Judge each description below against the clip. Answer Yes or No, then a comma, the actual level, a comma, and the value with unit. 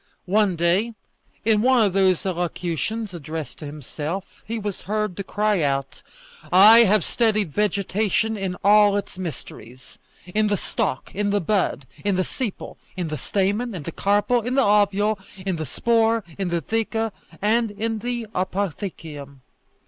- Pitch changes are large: No, average, 3.7 semitones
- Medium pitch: No, high, 200 Hz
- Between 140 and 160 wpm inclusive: Yes, average, 155 wpm